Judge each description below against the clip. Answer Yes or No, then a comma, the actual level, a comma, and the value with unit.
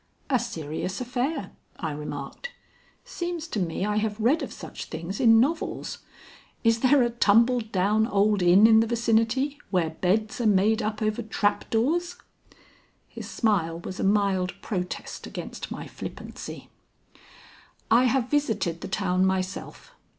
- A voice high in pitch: Yes, high, 215 Hz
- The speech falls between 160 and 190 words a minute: No, average, 145 wpm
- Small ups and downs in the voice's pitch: No, average, 4.3 semitones